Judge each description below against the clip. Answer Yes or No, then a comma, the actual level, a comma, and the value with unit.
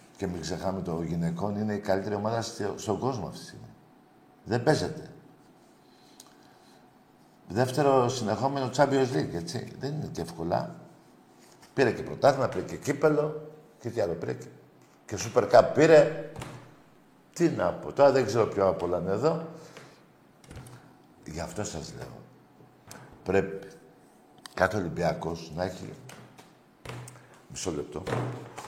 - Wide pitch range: Yes, wide, 7.5 semitones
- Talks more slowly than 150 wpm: Yes, average, 130 wpm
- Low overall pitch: Yes, low, 110 Hz